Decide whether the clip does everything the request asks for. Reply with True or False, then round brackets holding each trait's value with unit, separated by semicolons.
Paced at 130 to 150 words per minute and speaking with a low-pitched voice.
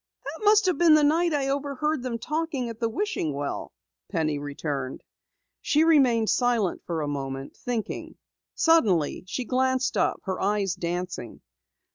False (145 wpm; 235 Hz)